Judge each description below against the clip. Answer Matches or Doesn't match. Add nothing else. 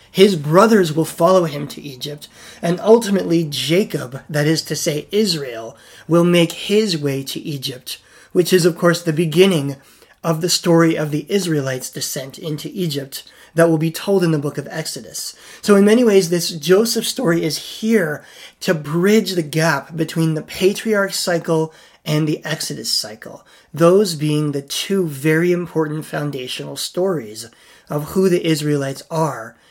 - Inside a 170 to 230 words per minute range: Doesn't match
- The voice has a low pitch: Doesn't match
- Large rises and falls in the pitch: Doesn't match